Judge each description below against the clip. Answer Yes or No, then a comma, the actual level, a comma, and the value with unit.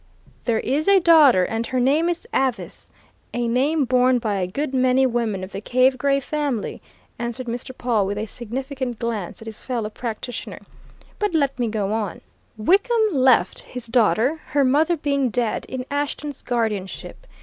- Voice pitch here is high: Yes, very high, 250 Hz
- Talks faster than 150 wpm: Yes, average, 170 wpm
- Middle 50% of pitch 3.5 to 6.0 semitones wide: Yes, average, 3.8 semitones